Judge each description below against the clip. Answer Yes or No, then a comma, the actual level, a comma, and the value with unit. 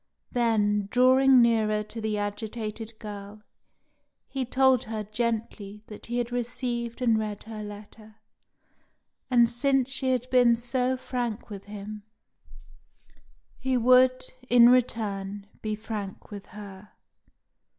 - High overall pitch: Yes, high, 225 Hz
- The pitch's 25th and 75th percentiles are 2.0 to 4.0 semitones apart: Yes, average, 2.8 semitones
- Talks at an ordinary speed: No, slow, 120 wpm